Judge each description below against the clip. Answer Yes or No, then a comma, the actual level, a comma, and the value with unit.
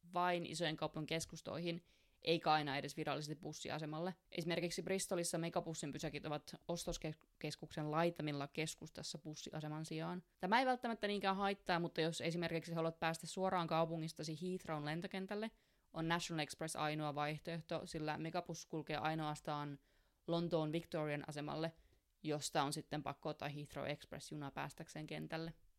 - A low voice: No, medium, 160 Hz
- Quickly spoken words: No, average, 125 wpm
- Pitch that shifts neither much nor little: No, narrow, 2.2 semitones